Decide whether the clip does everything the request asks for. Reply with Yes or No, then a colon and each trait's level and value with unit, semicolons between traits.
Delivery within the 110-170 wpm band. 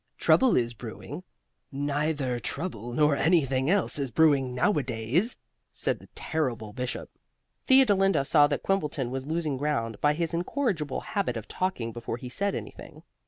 Yes: average, 150 wpm